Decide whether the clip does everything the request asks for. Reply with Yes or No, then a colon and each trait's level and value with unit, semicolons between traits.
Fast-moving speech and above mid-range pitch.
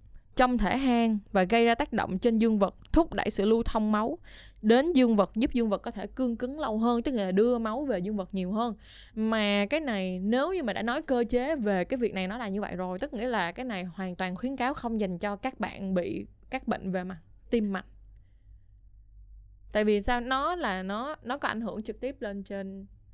No: average, 240 wpm; high, 215 Hz